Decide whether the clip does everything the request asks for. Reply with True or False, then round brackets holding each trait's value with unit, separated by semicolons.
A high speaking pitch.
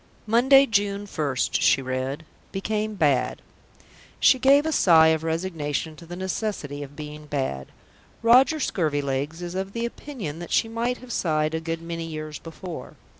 False (165 Hz)